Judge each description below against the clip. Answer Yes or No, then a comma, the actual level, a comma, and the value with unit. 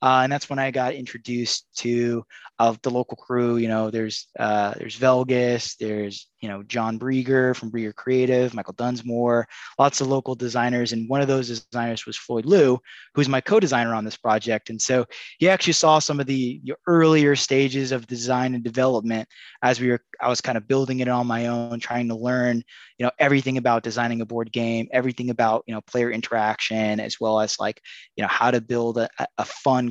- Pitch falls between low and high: No, low, 120 Hz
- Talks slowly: No, fast, 205 wpm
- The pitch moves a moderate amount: No, narrow, 2.1 semitones